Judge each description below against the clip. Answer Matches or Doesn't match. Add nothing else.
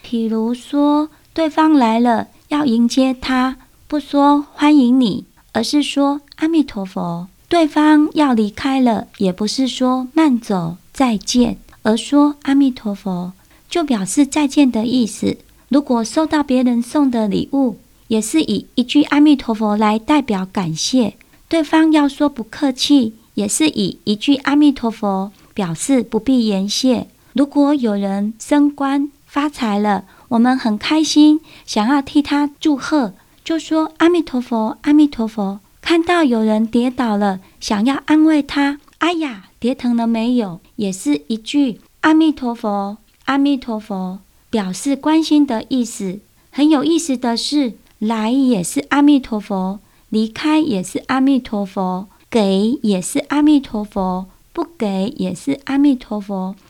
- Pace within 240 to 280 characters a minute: Doesn't match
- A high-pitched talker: Matches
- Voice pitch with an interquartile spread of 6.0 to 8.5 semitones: Doesn't match